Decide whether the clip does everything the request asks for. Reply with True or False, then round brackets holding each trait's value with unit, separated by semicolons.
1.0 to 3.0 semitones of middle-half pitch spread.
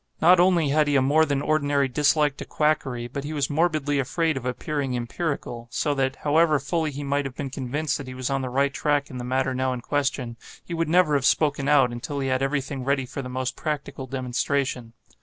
True (2.4 semitones)